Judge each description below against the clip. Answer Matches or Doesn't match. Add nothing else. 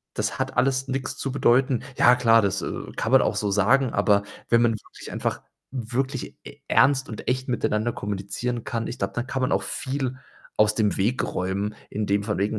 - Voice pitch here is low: Matches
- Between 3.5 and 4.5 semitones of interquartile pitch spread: Matches